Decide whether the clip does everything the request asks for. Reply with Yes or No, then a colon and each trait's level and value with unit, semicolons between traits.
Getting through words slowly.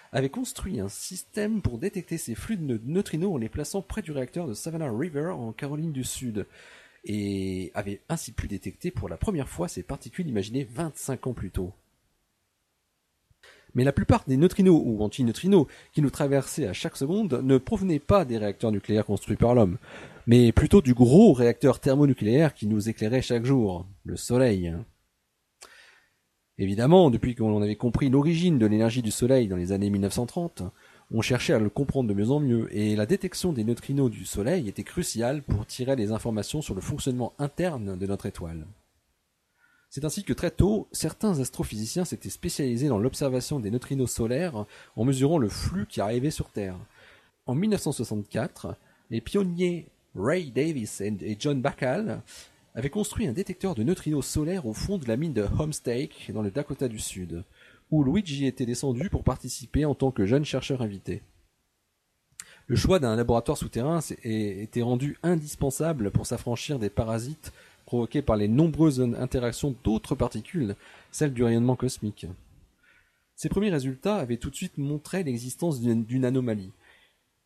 No: average, 165 wpm